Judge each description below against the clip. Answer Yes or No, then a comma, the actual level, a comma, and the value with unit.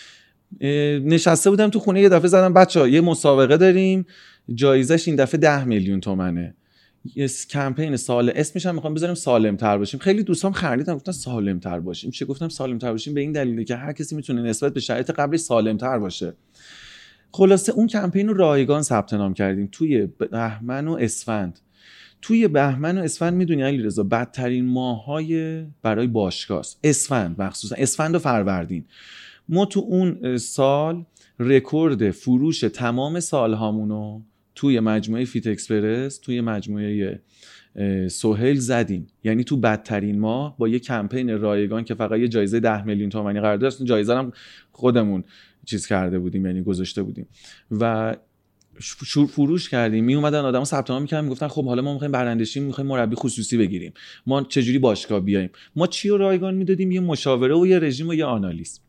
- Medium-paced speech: No, fast, 165 wpm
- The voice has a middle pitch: No, low, 125 Hz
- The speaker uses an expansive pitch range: Yes, wide, 6.1 semitones